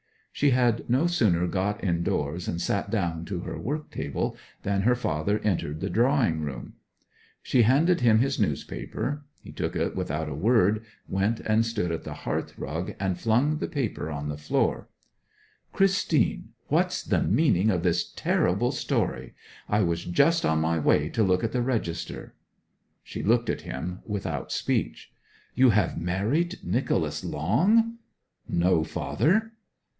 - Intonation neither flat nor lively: No, wide, 6.7 semitones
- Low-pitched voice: Yes, low, 105 Hz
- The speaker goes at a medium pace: Yes, average, 150 wpm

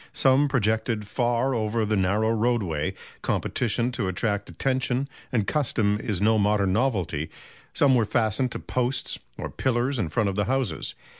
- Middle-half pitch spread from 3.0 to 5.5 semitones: Yes, average, 3.7 semitones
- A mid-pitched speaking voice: No, low, 115 Hz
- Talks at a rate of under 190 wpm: Yes, average, 155 wpm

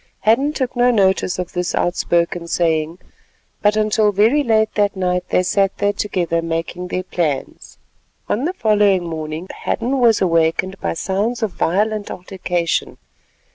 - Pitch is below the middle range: No, high, 190 Hz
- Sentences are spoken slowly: No, average, 145 wpm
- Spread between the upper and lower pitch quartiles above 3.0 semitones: Yes, average, 3.8 semitones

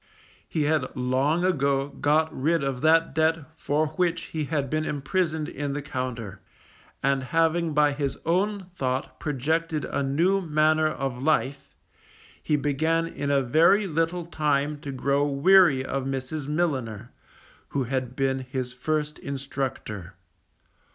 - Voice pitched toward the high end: No, medium, 145 Hz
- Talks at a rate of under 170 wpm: Yes, average, 140 wpm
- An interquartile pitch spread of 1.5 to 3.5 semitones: Yes, average, 2.9 semitones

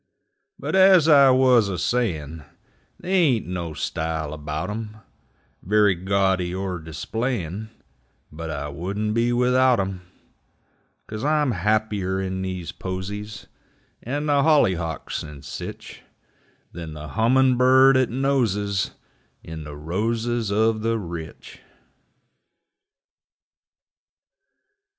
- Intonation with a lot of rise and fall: Yes, wide, 6.1 semitones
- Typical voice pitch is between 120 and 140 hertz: No, low, 105 Hz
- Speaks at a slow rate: Yes, slow, 110 wpm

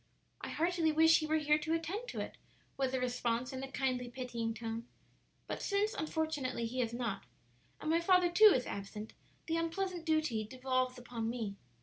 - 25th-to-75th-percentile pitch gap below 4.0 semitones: No, average, 5.2 semitones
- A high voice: Yes, very high, 265 Hz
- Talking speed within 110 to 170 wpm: No, average, 185 wpm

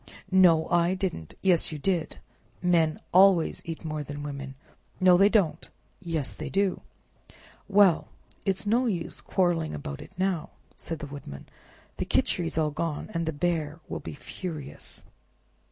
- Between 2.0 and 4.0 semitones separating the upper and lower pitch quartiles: Yes, average, 3.6 semitones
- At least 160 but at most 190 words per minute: No, average, 145 wpm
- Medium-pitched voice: Yes, medium, 165 Hz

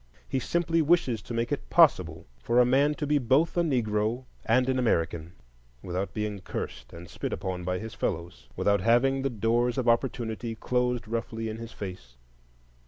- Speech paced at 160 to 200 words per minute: Yes, average, 175 wpm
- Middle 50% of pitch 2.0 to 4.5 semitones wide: No, average, 5.0 semitones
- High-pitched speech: No, low, 115 Hz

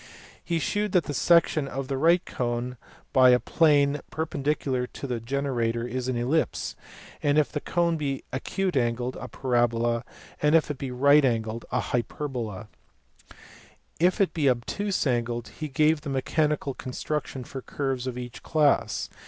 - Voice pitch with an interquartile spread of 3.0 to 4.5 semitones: Yes, average, 3.7 semitones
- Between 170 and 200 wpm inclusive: No, average, 160 wpm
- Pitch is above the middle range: No, low, 135 Hz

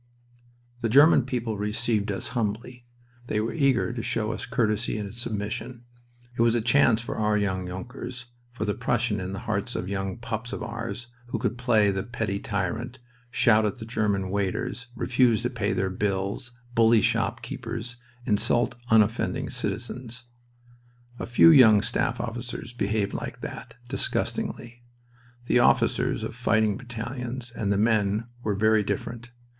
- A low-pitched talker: Yes, low, 115 Hz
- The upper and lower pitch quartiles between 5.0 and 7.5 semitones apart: No, average, 2.8 semitones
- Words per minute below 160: Yes, average, 150 wpm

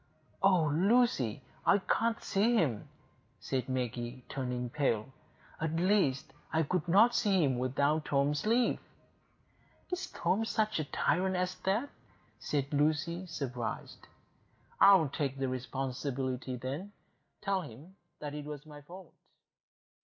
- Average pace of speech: No, slow, 120 wpm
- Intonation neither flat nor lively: No, wide, 6.2 semitones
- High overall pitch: No, medium, 150 Hz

